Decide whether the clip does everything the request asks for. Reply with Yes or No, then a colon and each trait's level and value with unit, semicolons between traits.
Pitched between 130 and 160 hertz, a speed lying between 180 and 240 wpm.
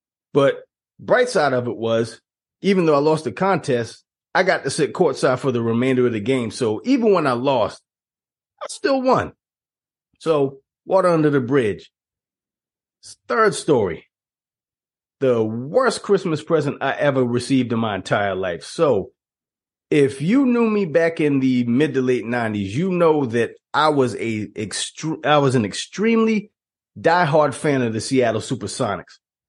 No: medium, 140 Hz; average, 160 wpm